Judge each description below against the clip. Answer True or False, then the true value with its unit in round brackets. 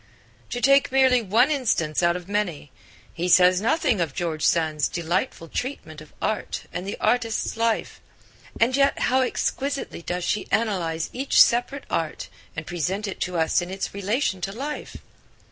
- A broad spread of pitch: True (6.4 semitones)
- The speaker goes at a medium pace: True (160 wpm)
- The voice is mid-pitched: False (195 Hz)